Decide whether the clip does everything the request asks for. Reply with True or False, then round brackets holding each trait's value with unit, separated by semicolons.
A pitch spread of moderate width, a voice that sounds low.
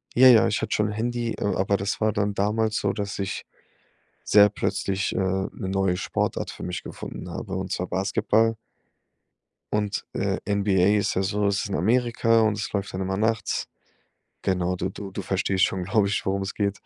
False (1.8 semitones; 100 Hz)